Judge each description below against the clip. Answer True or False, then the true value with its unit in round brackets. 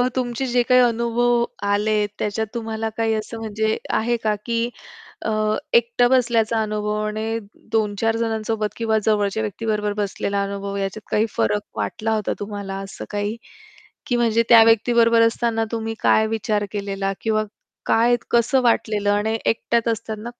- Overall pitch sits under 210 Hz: False (220 Hz)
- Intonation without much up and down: True (1.7 semitones)